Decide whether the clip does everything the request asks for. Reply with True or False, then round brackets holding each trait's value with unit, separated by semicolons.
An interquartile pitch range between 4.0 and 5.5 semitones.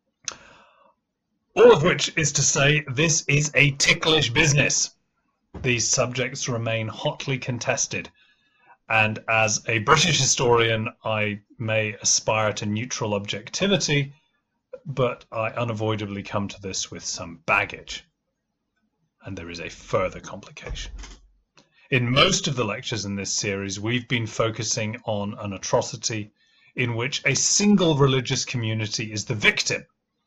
True (4.7 semitones)